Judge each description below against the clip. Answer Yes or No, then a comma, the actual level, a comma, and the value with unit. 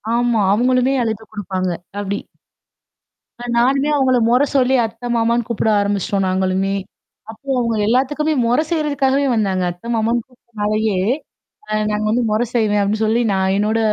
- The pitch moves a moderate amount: Yes, average, 3.3 semitones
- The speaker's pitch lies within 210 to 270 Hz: Yes, high, 225 Hz